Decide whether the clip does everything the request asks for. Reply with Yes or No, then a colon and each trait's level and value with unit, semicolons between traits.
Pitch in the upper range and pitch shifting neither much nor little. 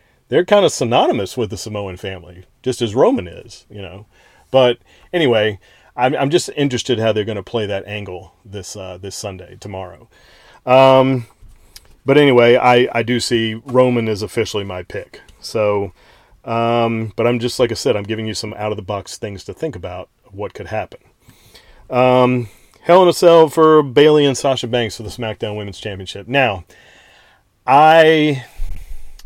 No: low, 110 Hz; average, 4.1 semitones